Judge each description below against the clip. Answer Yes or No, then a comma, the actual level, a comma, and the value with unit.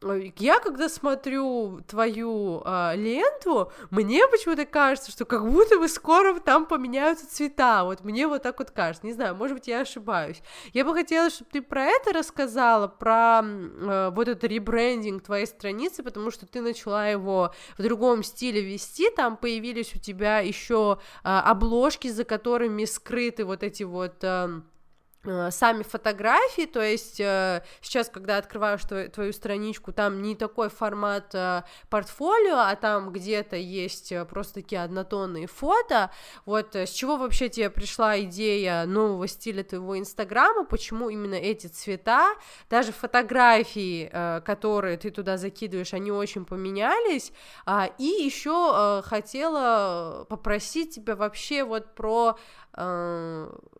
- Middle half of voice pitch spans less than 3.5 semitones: No, average, 4.2 semitones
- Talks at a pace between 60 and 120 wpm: No, average, 135 wpm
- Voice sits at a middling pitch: No, high, 220 Hz